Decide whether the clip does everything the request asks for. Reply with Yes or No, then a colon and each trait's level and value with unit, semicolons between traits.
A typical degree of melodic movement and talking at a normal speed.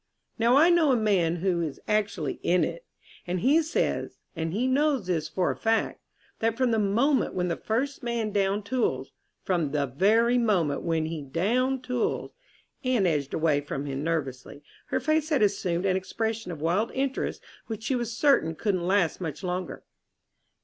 No: wide, 6.6 semitones; average, 175 wpm